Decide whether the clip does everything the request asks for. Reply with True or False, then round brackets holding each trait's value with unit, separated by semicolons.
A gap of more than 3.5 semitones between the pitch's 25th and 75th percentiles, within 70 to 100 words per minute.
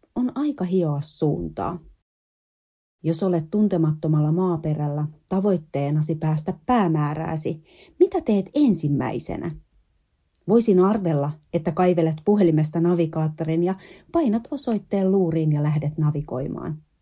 True (4.0 semitones; 95 wpm)